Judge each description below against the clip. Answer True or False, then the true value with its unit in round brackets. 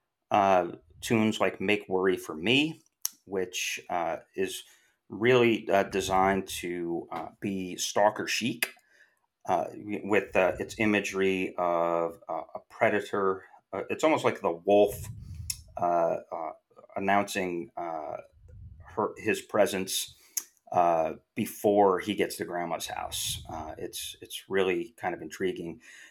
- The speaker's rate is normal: False (125 wpm)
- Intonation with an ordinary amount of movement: False (1.9 semitones)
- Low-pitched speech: True (95 Hz)